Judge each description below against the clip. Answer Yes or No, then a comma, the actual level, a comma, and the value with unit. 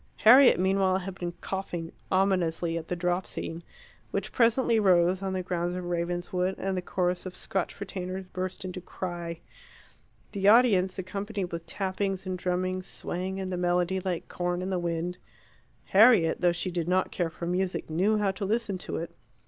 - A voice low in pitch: No, medium, 185 Hz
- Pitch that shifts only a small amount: Yes, narrow, 1.6 semitones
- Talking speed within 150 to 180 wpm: Yes, average, 175 wpm